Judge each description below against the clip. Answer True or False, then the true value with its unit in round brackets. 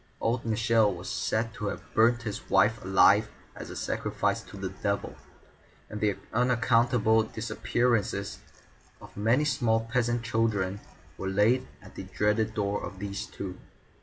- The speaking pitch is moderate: False (110 Hz)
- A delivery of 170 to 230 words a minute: False (145 wpm)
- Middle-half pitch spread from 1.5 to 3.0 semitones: True (2.6 semitones)